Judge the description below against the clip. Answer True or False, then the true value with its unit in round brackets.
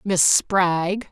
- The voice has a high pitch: False (180 Hz)